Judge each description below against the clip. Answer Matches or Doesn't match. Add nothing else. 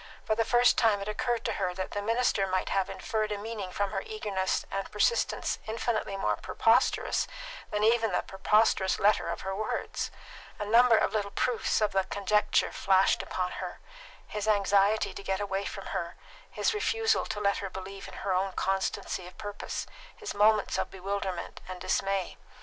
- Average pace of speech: Matches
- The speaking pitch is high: Matches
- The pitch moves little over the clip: Matches